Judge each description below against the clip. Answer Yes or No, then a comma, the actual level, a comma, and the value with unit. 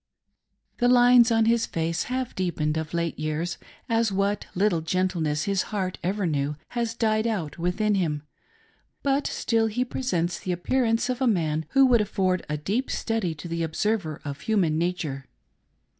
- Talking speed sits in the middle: Yes, average, 175 wpm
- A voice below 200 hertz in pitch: Yes, medium, 185 Hz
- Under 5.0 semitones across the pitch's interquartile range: No, wide, 5.6 semitones